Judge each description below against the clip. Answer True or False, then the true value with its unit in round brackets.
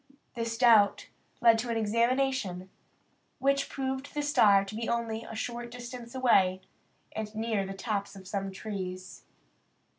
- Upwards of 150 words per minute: False (145 wpm)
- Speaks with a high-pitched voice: True (225 Hz)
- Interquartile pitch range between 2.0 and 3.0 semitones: False (3.5 semitones)